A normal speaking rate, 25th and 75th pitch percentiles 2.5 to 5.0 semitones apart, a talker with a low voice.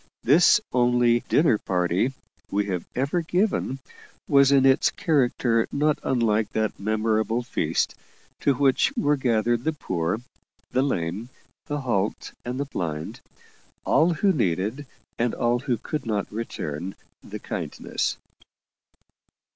No: slow, 125 wpm; average, 4.6 semitones; low, 120 Hz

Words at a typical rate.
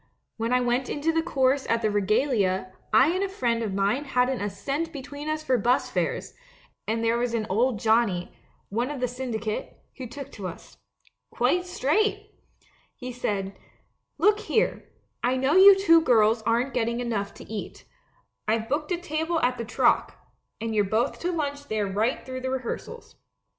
Yes: average, 185 wpm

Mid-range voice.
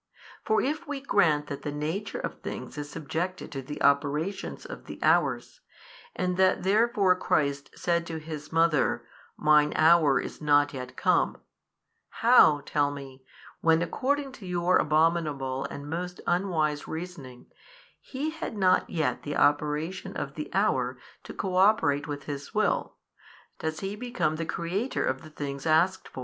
Yes: medium, 160 Hz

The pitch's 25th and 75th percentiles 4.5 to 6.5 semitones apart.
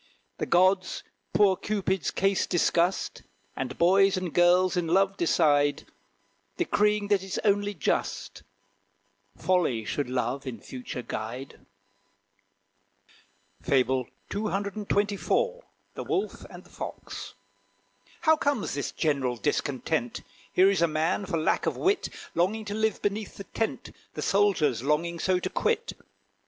Yes: wide, 5.4 semitones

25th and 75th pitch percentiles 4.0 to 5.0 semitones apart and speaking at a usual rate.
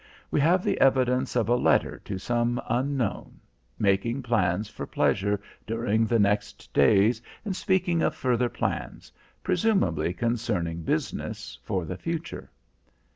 No: average, 4.7 semitones; slow, 130 wpm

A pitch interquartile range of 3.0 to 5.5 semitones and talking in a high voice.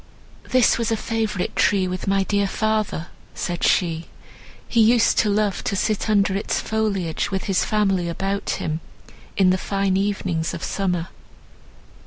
No: narrow, 2.6 semitones; high, 195 Hz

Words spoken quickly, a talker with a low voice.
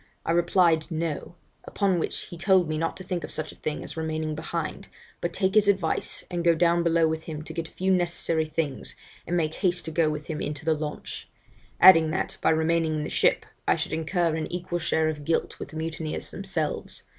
No: fast, 220 wpm; medium, 165 Hz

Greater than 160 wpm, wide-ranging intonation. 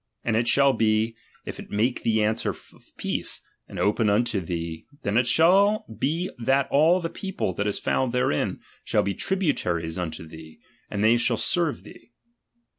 Yes: average, 175 wpm; wide, 5.7 semitones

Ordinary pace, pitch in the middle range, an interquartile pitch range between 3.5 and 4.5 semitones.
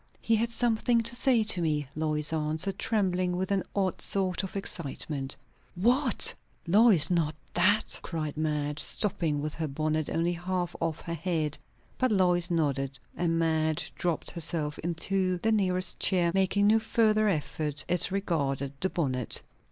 Yes: average, 150 wpm; medium, 175 Hz; average, 4.2 semitones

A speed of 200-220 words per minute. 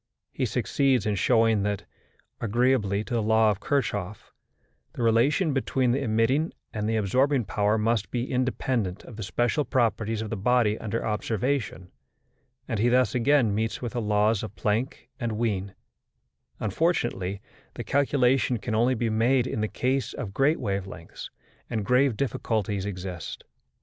No: average, 160 wpm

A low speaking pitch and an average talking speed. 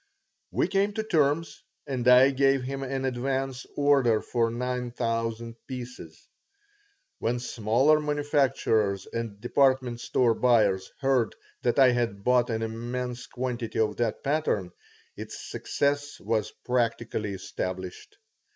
No: low, 125 Hz; slow, 125 wpm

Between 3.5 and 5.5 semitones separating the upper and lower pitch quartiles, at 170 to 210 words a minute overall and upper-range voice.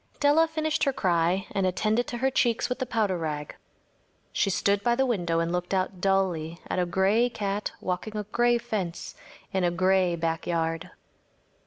Yes: average, 5.2 semitones; average, 175 wpm; high, 195 Hz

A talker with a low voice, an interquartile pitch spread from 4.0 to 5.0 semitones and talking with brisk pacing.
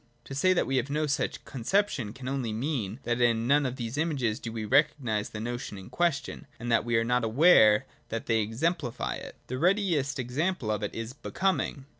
Yes: low, 125 Hz; average, 4.5 semitones; fast, 210 wpm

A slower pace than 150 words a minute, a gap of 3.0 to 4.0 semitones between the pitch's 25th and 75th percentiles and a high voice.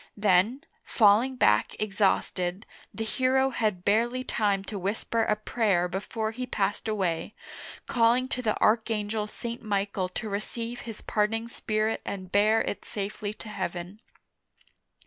No: slow, 135 wpm; narrow, 2.5 semitones; high, 215 Hz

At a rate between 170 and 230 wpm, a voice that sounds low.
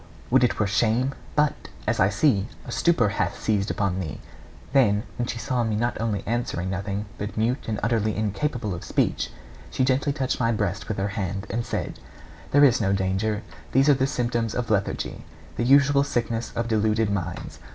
Yes: average, 190 wpm; low, 110 Hz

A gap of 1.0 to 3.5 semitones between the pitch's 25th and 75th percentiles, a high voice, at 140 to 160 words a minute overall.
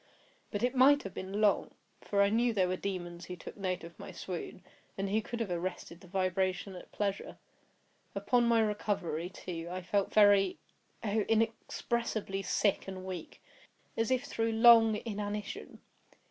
Yes: average, 3.2 semitones; high, 200 Hz; average, 155 wpm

